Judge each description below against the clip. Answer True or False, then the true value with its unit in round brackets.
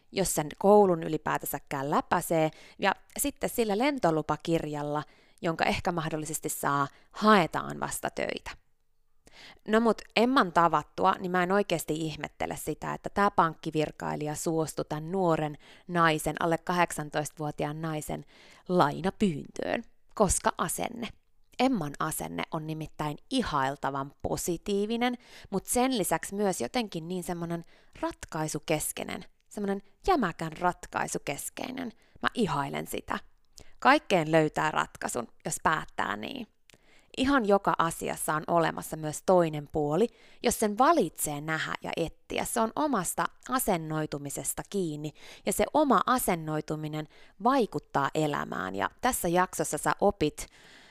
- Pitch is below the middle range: False (170 Hz)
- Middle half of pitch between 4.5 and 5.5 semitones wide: True (5.0 semitones)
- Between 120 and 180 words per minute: False (110 wpm)